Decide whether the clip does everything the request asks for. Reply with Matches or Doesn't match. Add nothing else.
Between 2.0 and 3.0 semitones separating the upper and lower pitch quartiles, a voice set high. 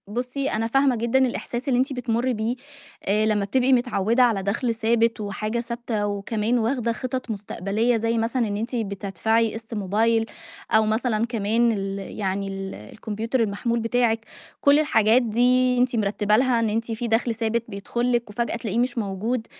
Matches